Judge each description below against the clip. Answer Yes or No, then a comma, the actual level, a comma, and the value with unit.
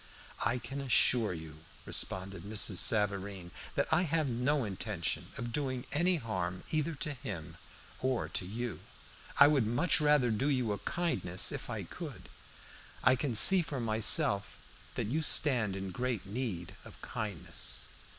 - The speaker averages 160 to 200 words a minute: No, average, 150 wpm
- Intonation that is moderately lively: No, wide, 6.2 semitones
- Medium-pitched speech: No, low, 120 Hz